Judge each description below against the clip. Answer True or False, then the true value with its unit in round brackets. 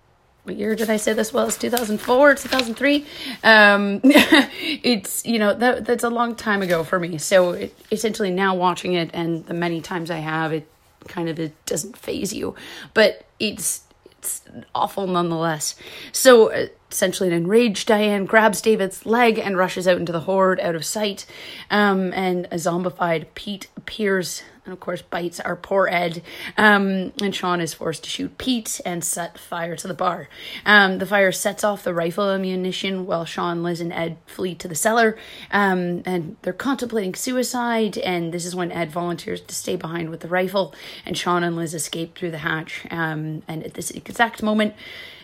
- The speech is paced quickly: False (185 wpm)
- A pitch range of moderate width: True (4.0 semitones)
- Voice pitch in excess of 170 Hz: True (185 Hz)